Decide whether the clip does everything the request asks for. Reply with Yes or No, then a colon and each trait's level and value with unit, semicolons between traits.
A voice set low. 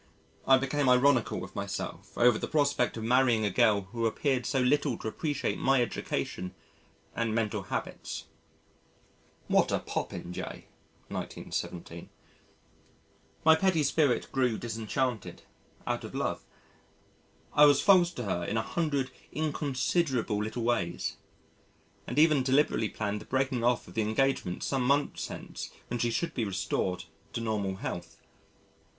Yes: low, 125 Hz